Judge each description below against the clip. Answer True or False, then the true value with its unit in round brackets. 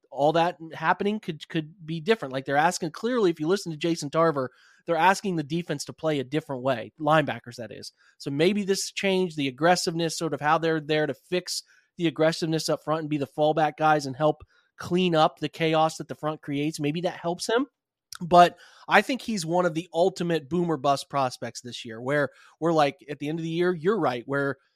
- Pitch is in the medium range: True (160 Hz)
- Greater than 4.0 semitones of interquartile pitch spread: False (3.1 semitones)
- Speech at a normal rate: False (220 wpm)